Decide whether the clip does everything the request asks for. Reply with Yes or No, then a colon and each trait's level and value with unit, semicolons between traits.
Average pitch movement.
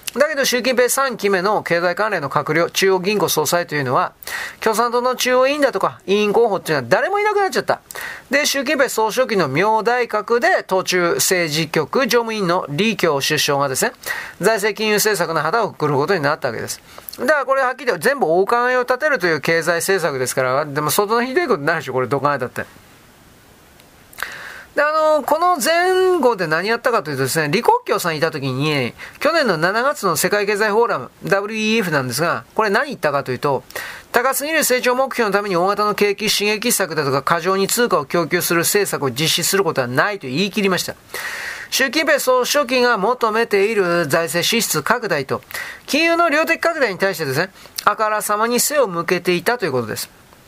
No: wide, 6.7 semitones